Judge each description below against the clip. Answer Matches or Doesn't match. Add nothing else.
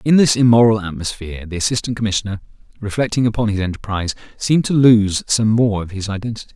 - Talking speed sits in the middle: Matches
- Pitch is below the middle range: Matches